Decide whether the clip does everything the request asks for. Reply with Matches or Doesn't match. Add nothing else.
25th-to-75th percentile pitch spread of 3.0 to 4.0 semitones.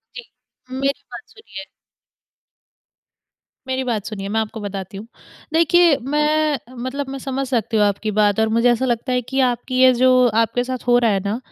Matches